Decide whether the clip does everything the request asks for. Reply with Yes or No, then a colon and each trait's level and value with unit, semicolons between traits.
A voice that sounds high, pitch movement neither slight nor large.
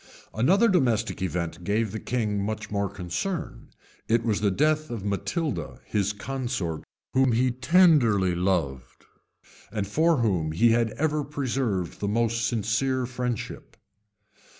No: low, 115 Hz; average, 4.9 semitones